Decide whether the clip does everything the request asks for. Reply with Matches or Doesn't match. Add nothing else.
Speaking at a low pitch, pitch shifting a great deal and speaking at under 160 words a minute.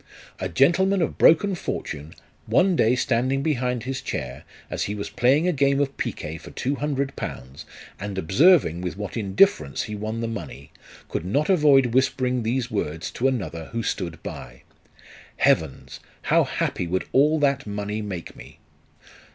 Doesn't match